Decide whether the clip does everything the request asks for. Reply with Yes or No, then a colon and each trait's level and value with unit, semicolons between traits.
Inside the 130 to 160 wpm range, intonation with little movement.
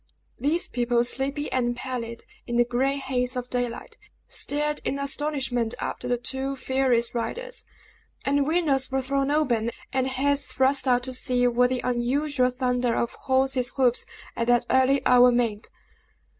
Yes: average, 155 wpm; narrow, 2.0 semitones